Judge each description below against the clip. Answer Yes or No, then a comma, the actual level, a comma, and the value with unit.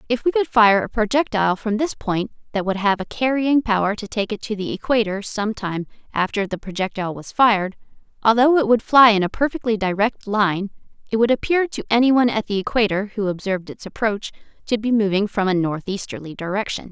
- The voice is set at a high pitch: Yes, high, 215 Hz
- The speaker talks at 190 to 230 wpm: Yes, average, 200 wpm